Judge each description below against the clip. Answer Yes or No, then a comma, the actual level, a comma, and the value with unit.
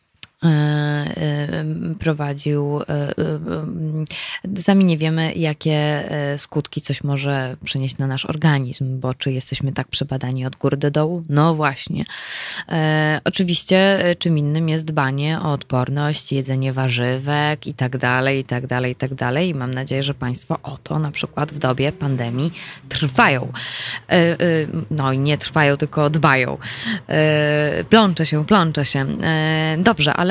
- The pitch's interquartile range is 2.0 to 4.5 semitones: Yes, average, 2.9 semitones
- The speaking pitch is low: No, medium, 150 Hz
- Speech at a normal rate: Yes, average, 145 wpm